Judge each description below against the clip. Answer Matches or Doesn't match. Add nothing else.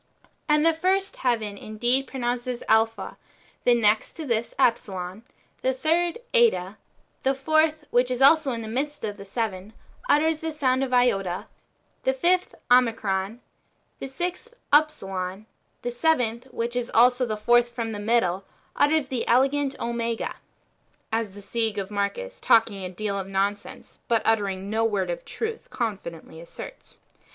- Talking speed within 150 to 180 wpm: Matches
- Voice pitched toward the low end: Doesn't match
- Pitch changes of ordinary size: Matches